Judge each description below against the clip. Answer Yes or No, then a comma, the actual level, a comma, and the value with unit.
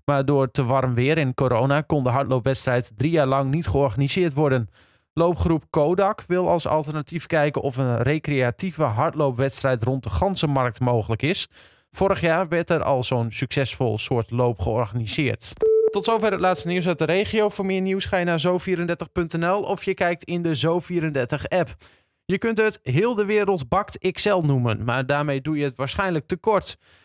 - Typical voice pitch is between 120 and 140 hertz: No, medium, 150 Hz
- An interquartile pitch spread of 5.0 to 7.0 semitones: Yes, wide, 5.4 semitones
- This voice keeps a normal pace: Yes, average, 175 wpm